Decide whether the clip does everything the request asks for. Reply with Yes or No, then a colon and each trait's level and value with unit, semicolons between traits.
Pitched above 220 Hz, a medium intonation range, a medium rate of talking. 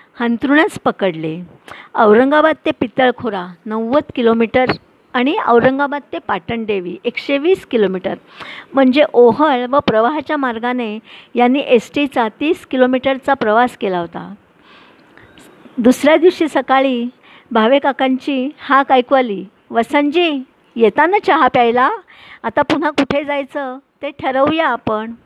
Yes: very high, 255 Hz; average, 3.8 semitones; average, 105 wpm